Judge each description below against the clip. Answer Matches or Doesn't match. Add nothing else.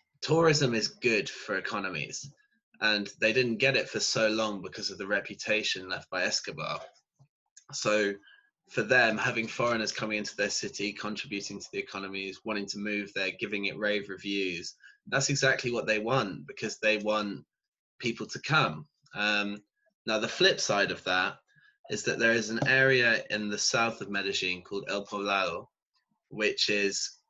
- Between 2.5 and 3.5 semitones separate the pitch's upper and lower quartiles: Doesn't match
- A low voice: Matches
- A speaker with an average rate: Matches